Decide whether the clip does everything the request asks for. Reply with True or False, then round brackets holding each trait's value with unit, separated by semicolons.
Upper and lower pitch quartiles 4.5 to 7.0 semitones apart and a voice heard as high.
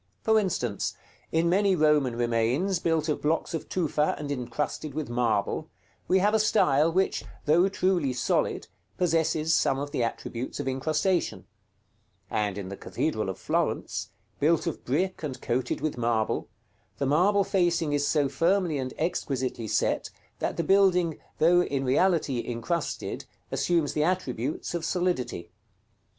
False (5.4 semitones; 155 Hz)